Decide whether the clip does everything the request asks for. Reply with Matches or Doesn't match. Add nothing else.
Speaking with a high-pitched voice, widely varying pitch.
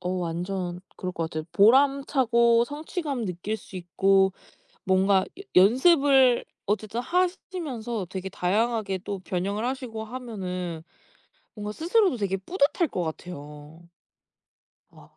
Matches